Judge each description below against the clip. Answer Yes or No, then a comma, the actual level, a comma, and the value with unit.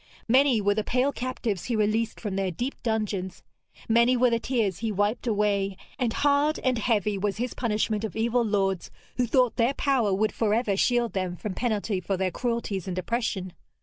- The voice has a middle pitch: No, high, 220 Hz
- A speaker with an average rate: Yes, average, 190 wpm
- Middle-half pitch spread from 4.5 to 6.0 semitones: No, average, 3.4 semitones